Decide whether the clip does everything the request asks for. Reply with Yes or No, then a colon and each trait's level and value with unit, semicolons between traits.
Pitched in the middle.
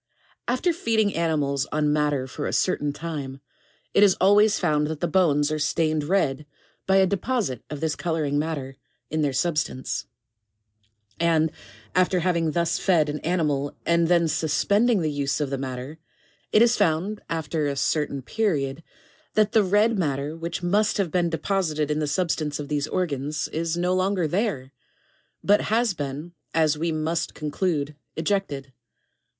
Yes: medium, 160 Hz